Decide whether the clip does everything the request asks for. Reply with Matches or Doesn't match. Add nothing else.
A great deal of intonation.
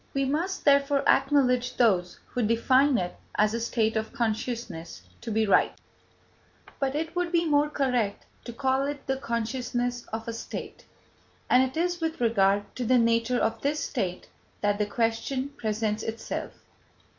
Doesn't match